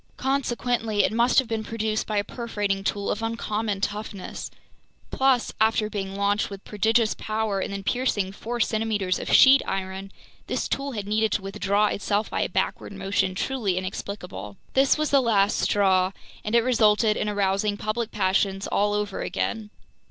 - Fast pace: No, average, 165 wpm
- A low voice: No, high, 210 Hz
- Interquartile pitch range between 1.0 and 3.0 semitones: Yes, narrow, 2.4 semitones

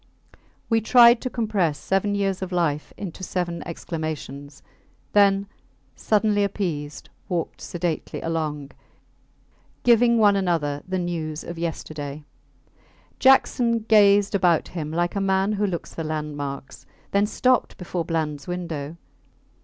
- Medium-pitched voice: Yes, medium, 175 Hz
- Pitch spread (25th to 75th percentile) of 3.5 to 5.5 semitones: Yes, average, 4.5 semitones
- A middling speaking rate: No, slow, 120 wpm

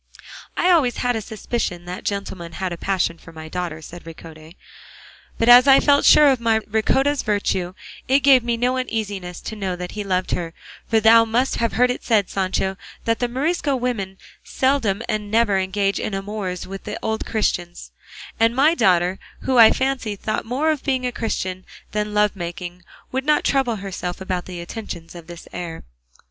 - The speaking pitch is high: Yes, high, 210 Hz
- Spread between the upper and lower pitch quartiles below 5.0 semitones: No, average, 5.3 semitones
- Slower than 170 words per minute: No, average, 185 wpm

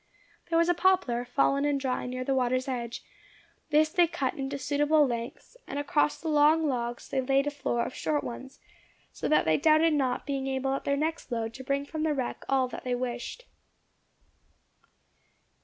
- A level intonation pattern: No, average, 3.0 semitones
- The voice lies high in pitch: Yes, very high, 275 Hz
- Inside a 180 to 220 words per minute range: Yes, average, 190 wpm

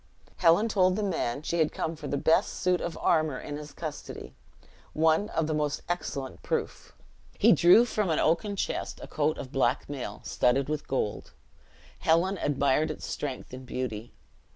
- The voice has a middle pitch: Yes, medium, 155 Hz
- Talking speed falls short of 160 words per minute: No, average, 170 wpm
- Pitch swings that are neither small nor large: Yes, average, 3.7 semitones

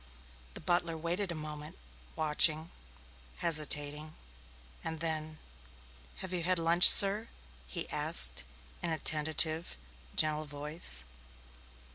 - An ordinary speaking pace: No, slow, 105 wpm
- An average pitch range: No, narrow, 2.0 semitones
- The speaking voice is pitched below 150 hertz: No, medium, 155 Hz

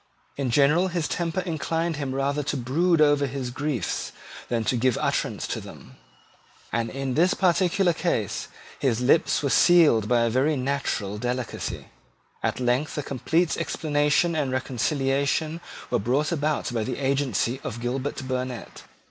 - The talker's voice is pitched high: No, medium, 140 Hz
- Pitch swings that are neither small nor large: Yes, average, 3.7 semitones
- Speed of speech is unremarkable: Yes, average, 150 wpm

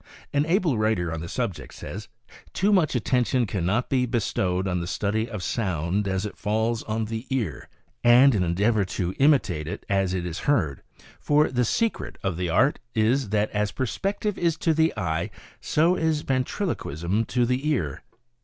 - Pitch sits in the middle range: No, low, 110 Hz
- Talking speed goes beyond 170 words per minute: Yes, average, 185 wpm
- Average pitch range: No, wide, 6.4 semitones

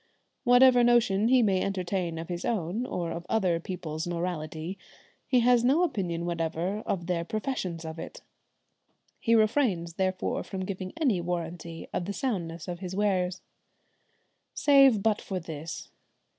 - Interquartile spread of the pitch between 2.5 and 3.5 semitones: No, average, 4.7 semitones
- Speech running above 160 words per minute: No, average, 145 wpm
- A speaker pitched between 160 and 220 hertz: Yes, medium, 185 Hz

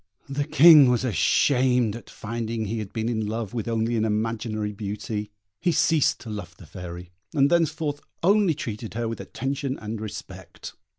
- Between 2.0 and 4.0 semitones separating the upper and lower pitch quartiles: No, average, 4.4 semitones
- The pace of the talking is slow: No, average, 170 wpm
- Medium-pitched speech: No, low, 115 Hz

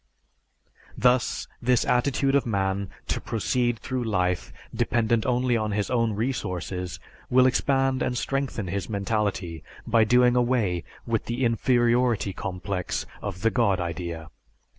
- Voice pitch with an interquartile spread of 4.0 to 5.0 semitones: Yes, average, 4.3 semitones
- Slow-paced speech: Yes, slow, 130 wpm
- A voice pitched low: Yes, low, 115 Hz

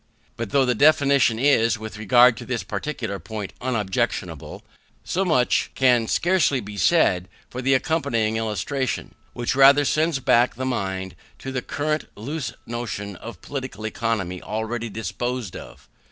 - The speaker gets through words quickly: No, average, 145 wpm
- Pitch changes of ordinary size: Yes, average, 3.8 semitones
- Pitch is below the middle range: Yes, low, 120 Hz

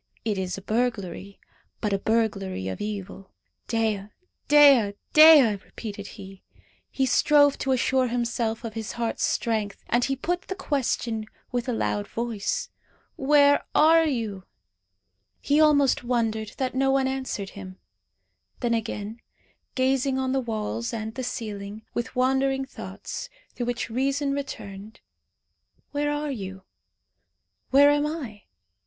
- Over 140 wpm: No, slow, 135 wpm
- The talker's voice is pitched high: Yes, high, 235 Hz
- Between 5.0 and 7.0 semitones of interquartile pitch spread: No, average, 4.4 semitones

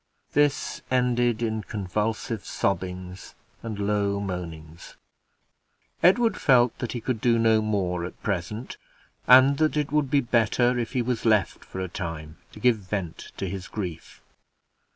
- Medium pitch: No, low, 110 Hz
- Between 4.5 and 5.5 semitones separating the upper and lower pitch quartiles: Yes, average, 4.9 semitones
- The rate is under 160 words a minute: Yes, average, 150 wpm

